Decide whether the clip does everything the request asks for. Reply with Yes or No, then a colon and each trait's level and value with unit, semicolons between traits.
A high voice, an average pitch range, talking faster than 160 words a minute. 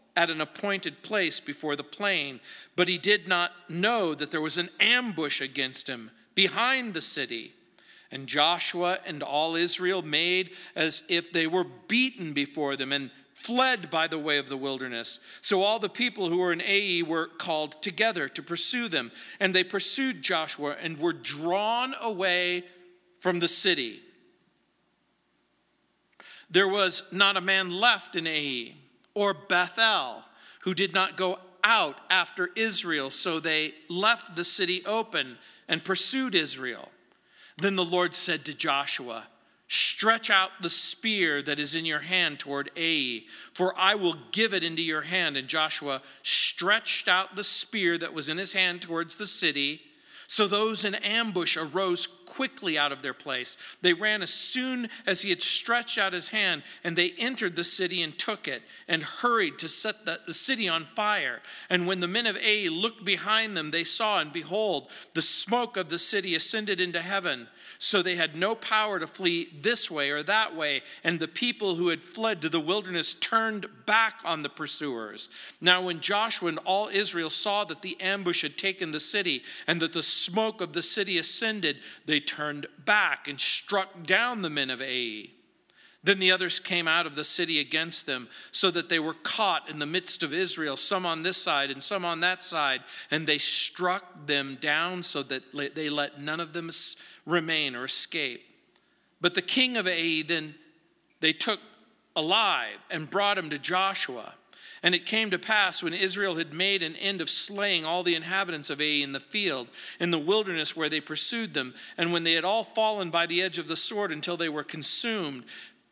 No: medium, 175 Hz; average, 4.1 semitones; average, 180 wpm